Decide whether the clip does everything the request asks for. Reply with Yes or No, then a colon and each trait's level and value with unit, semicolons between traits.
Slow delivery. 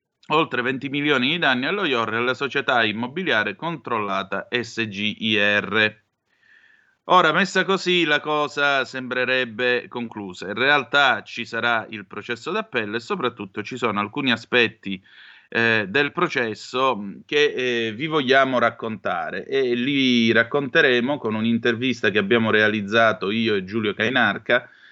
No: average, 125 wpm